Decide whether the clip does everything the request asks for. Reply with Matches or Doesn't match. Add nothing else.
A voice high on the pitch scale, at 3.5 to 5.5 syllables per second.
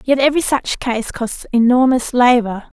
Matches